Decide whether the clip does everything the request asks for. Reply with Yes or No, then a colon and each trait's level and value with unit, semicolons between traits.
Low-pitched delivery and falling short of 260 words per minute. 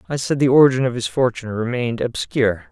Yes: low, 120 Hz; average, 200 wpm